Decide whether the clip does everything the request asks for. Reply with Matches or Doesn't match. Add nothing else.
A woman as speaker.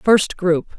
Matches